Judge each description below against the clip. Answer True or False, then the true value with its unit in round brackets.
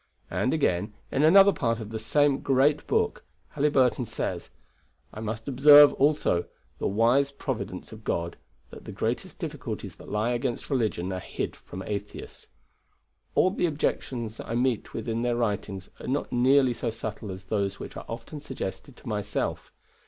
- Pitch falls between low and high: False (120 Hz)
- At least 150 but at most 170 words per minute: True (165 wpm)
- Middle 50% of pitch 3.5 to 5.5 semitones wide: True (4.8 semitones)